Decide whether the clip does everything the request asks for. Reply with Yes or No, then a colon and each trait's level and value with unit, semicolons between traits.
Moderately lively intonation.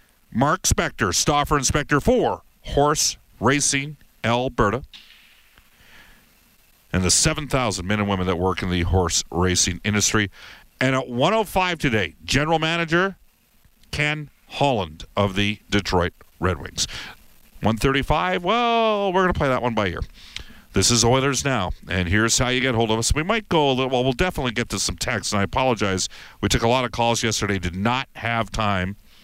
No: wide, 6.0 semitones